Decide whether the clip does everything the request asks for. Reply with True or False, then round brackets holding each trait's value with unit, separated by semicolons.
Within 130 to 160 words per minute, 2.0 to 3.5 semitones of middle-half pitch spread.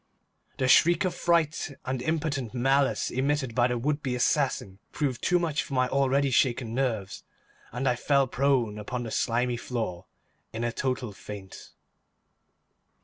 True (150 wpm; 2.8 semitones)